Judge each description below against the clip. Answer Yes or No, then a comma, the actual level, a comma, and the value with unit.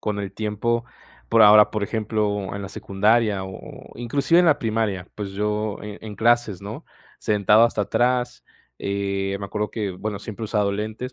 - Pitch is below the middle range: Yes, low, 105 Hz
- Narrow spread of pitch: Yes, narrow, 2.1 semitones